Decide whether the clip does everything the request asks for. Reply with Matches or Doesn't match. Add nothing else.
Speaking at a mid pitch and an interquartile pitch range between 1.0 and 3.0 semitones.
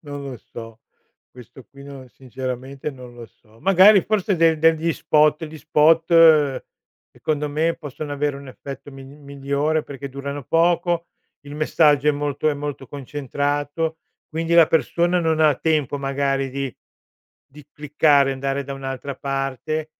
Matches